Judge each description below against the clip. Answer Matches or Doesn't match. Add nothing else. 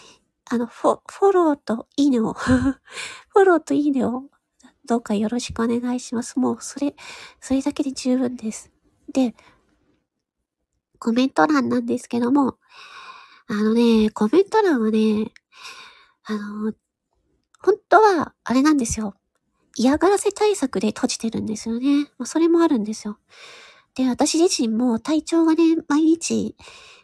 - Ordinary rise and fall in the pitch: Doesn't match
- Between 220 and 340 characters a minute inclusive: Matches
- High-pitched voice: Matches